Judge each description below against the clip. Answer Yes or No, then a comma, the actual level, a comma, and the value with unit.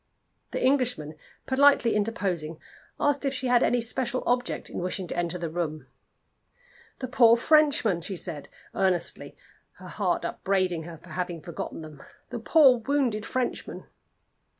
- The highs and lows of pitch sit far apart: Yes, wide, 6.8 semitones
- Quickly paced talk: No, average, 145 wpm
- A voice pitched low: No, high, 215 Hz